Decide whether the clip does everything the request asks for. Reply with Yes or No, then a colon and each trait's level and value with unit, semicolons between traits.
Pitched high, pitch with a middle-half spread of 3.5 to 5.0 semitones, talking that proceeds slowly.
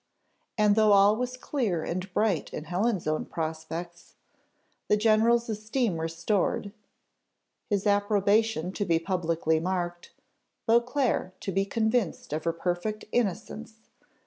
Yes: high, 200 Hz; average, 4.2 semitones; slow, 120 wpm